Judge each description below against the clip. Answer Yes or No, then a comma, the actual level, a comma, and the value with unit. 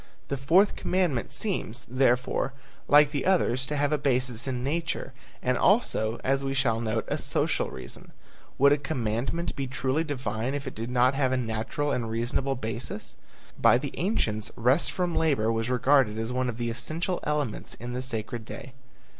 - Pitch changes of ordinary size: Yes, average, 3.6 semitones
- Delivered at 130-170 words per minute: No, average, 180 wpm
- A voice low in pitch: Yes, low, 130 Hz